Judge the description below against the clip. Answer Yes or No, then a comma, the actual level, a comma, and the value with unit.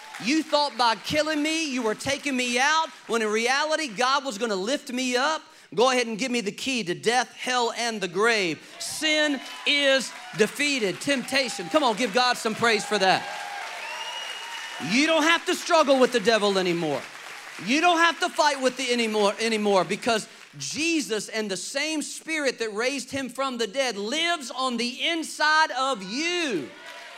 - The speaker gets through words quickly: No, average, 180 wpm